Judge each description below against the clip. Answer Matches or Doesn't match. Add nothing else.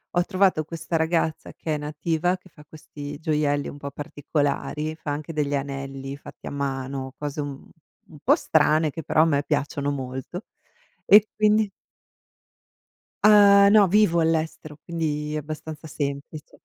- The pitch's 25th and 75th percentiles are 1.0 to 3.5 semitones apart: Matches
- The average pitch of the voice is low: Doesn't match